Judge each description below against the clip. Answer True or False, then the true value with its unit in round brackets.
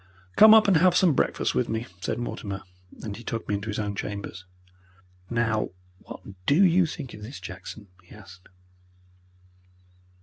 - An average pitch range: False (7.7 semitones)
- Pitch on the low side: True (110 Hz)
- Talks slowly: False (165 wpm)